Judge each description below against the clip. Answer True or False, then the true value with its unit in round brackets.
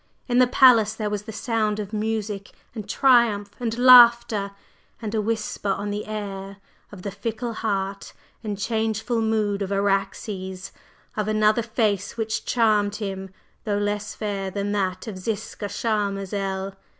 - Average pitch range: False (2.0 semitones)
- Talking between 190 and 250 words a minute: False (150 wpm)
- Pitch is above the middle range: True (210 Hz)